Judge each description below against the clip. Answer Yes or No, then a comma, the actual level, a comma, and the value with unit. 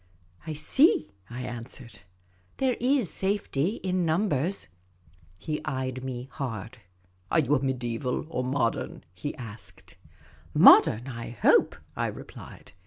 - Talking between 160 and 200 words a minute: No, average, 140 wpm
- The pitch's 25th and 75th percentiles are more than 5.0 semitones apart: Yes, wide, 5.5 semitones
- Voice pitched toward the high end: No, low, 130 Hz